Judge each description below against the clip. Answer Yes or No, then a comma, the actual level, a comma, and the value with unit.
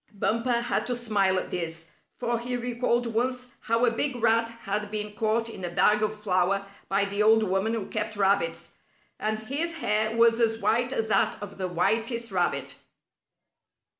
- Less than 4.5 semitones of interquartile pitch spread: Yes, average, 2.9 semitones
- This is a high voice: Yes, high, 220 Hz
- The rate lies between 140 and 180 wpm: Yes, average, 175 wpm